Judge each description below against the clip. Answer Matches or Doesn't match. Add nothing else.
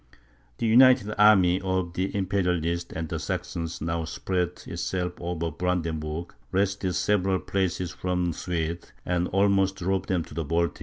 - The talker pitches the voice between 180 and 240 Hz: Doesn't match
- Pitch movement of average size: Doesn't match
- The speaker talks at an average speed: Matches